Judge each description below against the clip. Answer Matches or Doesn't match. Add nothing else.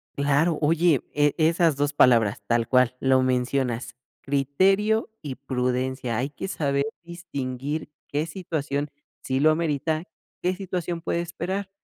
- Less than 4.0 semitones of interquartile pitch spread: Doesn't match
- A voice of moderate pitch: Matches